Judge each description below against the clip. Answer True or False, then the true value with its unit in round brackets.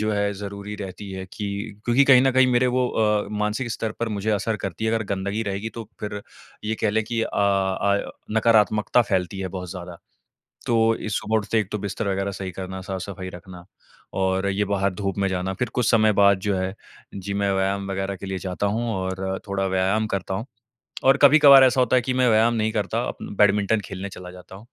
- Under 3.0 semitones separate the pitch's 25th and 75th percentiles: True (2.5 semitones)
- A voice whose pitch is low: True (100 Hz)